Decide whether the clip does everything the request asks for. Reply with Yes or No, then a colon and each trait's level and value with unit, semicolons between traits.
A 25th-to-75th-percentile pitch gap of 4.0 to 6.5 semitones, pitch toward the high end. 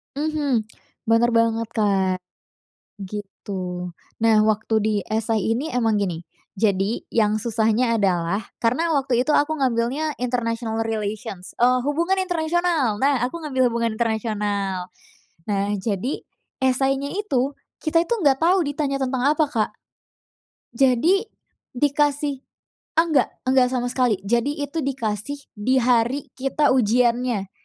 Yes: average, 4.6 semitones; high, 245 Hz